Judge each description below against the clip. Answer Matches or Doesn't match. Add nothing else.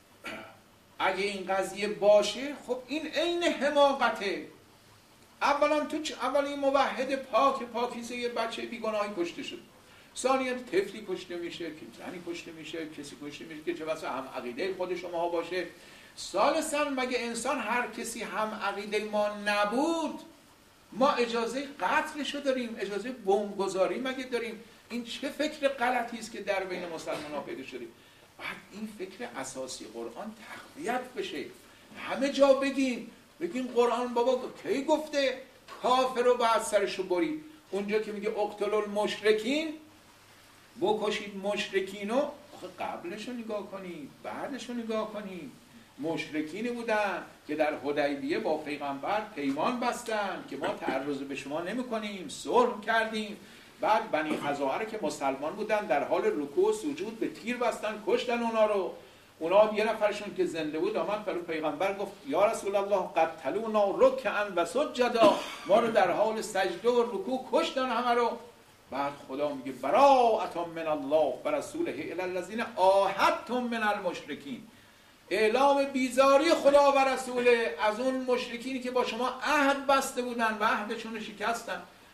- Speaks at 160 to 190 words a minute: Doesn't match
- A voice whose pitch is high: Matches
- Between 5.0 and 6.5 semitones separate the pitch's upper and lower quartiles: Matches